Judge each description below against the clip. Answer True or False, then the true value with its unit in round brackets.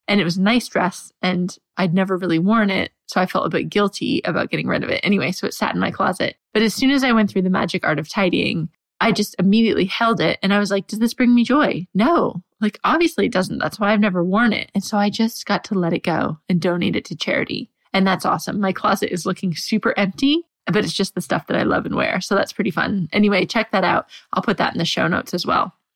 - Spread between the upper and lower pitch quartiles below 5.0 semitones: True (3.4 semitones)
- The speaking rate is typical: False (270 wpm)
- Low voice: False (200 Hz)